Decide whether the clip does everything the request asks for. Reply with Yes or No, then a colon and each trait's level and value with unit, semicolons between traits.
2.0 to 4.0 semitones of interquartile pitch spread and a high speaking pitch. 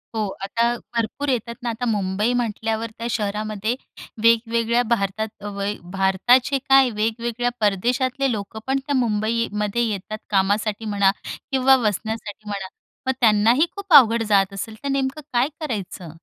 Yes: average, 2.9 semitones; high, 225 Hz